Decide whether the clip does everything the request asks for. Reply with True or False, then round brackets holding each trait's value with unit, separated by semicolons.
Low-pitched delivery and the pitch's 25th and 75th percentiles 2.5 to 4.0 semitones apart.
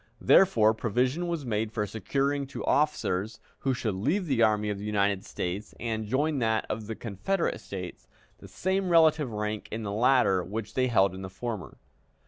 False (110 Hz; 5.0 semitones)